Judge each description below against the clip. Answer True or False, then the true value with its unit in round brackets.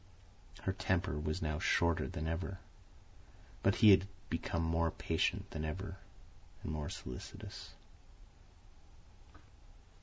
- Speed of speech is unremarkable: False (110 wpm)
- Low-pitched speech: True (80 Hz)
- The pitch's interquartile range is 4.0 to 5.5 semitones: False (3.5 semitones)